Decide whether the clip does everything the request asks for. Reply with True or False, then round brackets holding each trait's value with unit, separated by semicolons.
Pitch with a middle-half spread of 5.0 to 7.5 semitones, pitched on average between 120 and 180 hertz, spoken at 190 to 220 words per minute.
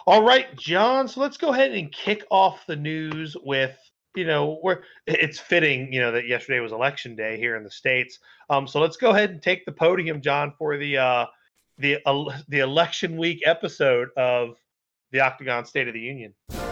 True (5.5 semitones; 150 Hz; 195 wpm)